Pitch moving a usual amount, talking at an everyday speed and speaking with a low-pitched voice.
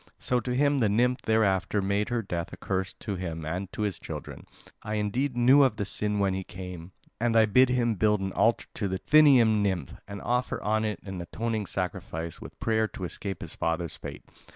No: average, 3.7 semitones; fast, 210 wpm; low, 105 Hz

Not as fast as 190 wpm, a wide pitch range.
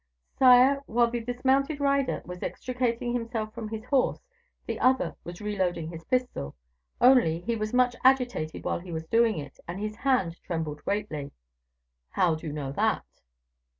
Yes: average, 160 wpm; wide, 6.6 semitones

